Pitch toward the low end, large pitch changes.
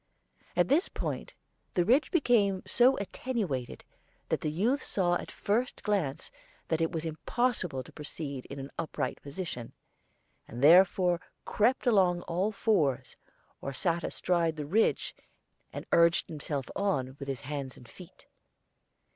No: medium, 170 Hz; wide, 6.1 semitones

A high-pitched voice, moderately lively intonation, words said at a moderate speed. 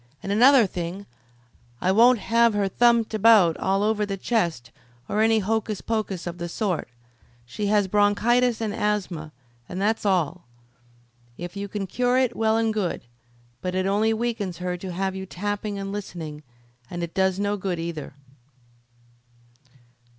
Yes: high, 200 Hz; average, 3.3 semitones; average, 160 wpm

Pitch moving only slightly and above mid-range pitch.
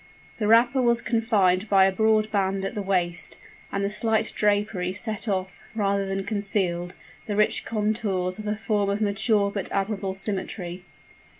Yes: narrow, 2.0 semitones; high, 200 Hz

